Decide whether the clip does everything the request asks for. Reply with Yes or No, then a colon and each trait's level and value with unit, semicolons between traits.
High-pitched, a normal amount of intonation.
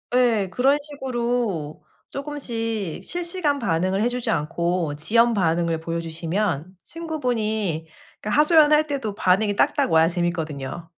No: high, 210 Hz; wide, 7.2 semitones